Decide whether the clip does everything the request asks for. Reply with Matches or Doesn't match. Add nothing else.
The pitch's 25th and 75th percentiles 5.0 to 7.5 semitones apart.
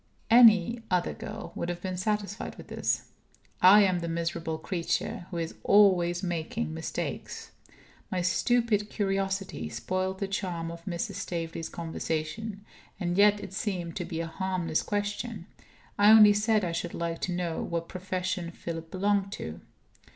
Doesn't match